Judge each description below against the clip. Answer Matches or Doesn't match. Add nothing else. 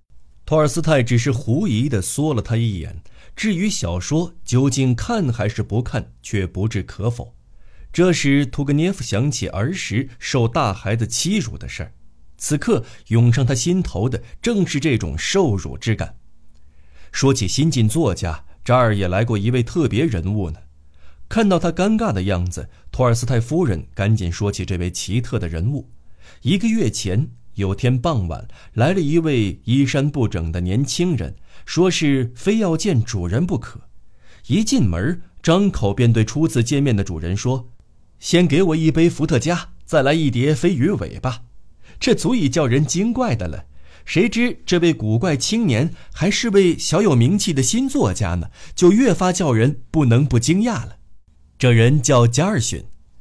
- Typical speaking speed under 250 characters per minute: Matches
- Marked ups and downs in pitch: Matches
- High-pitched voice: Doesn't match